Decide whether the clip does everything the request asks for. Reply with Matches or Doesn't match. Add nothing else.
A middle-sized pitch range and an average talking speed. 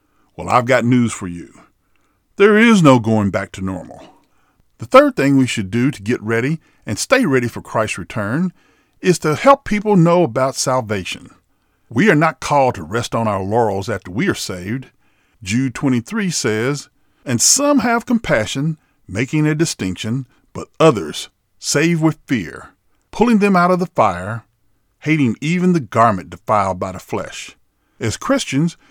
Doesn't match